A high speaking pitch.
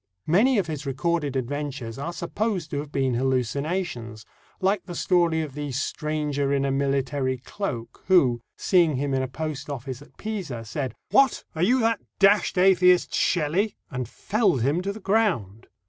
No: medium, 150 Hz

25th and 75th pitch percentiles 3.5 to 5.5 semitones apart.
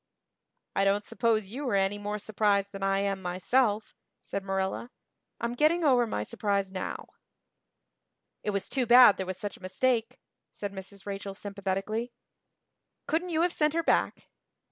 Yes: average, 3.8 semitones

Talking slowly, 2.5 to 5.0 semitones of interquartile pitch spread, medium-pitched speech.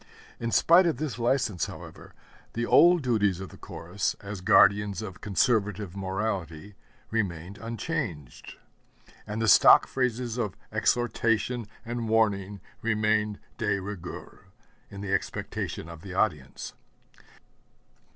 No: slow, 120 wpm; average, 3.4 semitones; low, 105 Hz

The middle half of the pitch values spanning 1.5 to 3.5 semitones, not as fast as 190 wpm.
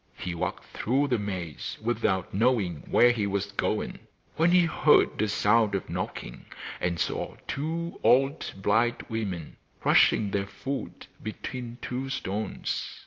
No: average, 4.7 semitones; average, 140 wpm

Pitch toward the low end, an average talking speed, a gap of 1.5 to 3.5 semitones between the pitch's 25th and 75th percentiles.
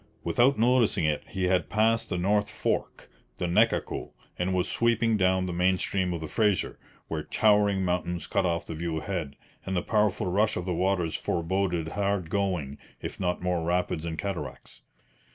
Yes: very low, 95 Hz; average, 175 wpm; average, 2.9 semitones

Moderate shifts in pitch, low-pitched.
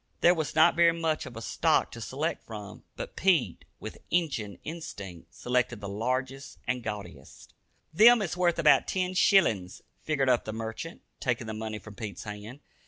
No: wide, 7.4 semitones; low, 125 Hz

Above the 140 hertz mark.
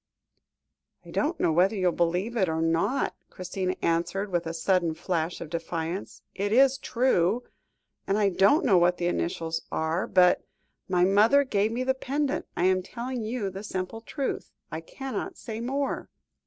Yes: high, 190 Hz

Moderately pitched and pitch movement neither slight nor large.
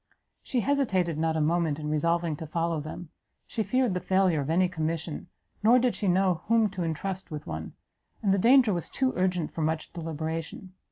Yes: medium, 175 Hz; average, 3.5 semitones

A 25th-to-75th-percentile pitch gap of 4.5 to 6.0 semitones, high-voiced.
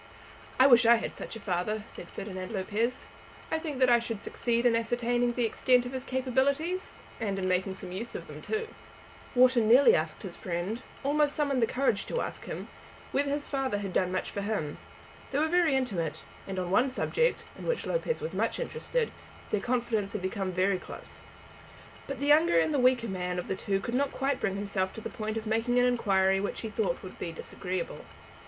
Yes: wide, 5.5 semitones; high, 235 Hz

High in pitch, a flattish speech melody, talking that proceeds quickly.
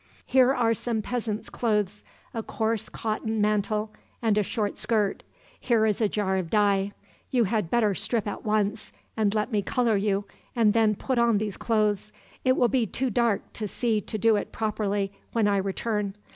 No: high, 215 Hz; narrow, 1.9 semitones; average, 185 wpm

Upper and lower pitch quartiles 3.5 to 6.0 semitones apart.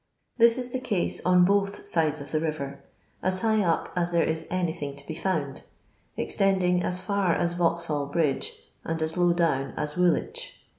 No: average, 3.0 semitones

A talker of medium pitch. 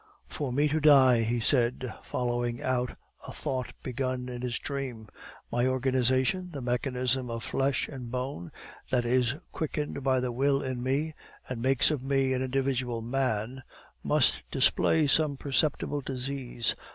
No: low, 130 Hz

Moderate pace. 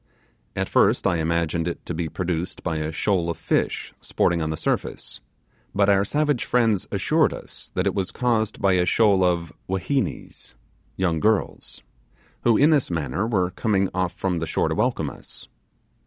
Yes: average, 175 wpm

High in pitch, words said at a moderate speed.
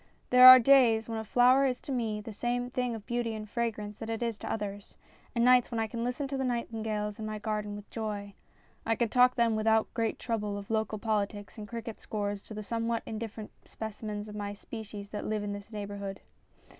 No: high, 220 Hz; fast, 220 wpm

